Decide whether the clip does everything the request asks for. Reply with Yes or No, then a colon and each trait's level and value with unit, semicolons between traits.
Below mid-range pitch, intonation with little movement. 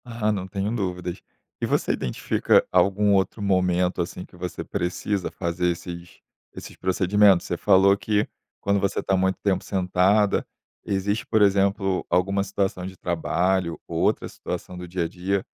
Yes: very low, 95 Hz; narrow, 1.8 semitones